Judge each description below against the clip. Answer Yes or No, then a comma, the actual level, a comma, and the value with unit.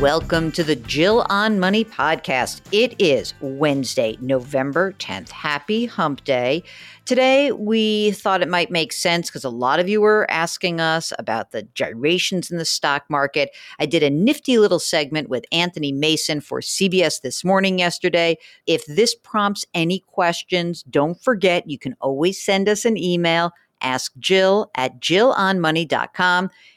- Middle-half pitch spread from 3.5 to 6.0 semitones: Yes, average, 4.8 semitones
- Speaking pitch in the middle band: Yes, medium, 170 Hz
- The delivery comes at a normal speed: Yes, average, 150 wpm